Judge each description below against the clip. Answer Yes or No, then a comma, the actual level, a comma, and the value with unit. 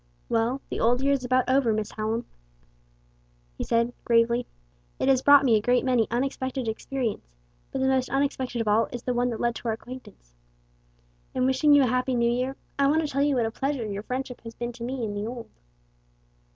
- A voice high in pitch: Yes, high, 245 Hz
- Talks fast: Yes, fast, 215 wpm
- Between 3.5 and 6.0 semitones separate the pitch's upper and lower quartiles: No, narrow, 2.5 semitones